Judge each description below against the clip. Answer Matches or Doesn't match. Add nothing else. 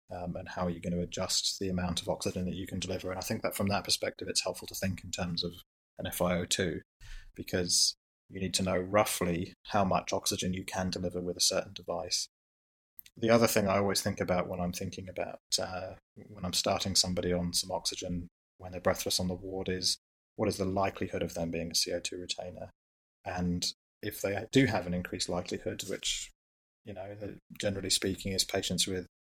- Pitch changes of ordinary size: Doesn't match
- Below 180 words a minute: Doesn't match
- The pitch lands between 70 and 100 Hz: Matches